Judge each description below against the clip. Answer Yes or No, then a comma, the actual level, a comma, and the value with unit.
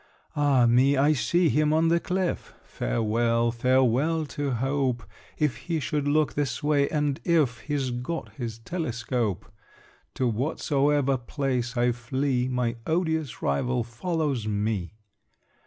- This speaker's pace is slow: Yes, slow, 130 wpm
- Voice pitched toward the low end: Yes, low, 130 Hz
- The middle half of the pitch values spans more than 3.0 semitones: Yes, average, 3.9 semitones